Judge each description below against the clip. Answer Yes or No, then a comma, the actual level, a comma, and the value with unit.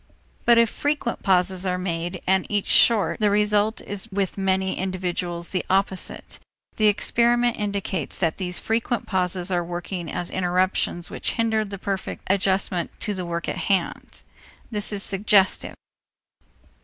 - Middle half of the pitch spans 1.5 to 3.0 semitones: Yes, narrow, 2.5 semitones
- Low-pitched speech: No, high, 190 Hz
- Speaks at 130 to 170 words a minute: Yes, average, 145 wpm